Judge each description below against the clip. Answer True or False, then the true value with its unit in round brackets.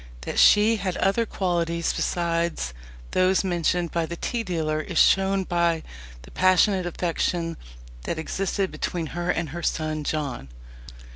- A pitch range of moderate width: False (2.3 semitones)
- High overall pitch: False (175 Hz)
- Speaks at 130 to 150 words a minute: True (140 wpm)